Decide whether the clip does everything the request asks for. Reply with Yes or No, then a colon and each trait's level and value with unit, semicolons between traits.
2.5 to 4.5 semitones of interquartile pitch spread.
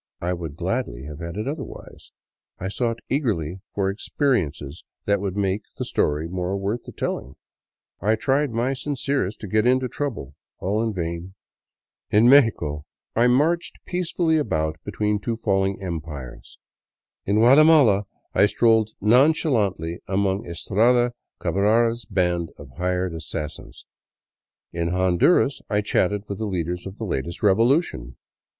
No: wide, 5.6 semitones